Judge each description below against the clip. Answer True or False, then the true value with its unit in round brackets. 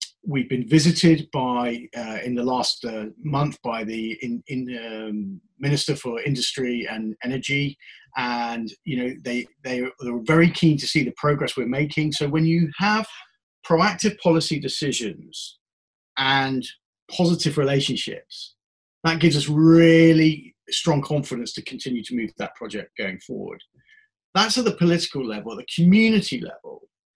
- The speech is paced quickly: False (145 wpm)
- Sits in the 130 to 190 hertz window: True (140 Hz)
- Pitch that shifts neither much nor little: True (4.9 semitones)